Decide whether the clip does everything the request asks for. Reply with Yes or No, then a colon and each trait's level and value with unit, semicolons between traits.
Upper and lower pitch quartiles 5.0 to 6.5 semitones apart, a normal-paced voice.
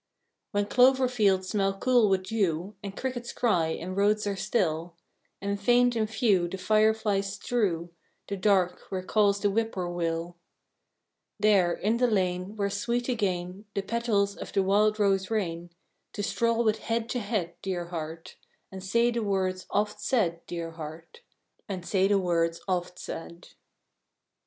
No: average, 3.4 semitones; average, 155 wpm